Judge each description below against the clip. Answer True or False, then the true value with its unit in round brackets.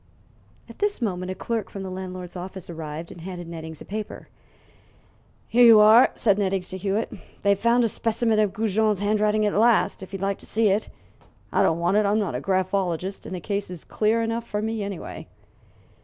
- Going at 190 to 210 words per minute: True (200 wpm)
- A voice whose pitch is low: False (200 Hz)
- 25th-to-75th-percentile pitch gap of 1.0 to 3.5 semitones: True (2.9 semitones)